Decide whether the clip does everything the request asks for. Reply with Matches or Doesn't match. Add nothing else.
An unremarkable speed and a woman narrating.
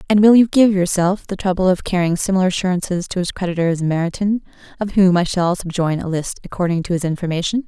Doesn't match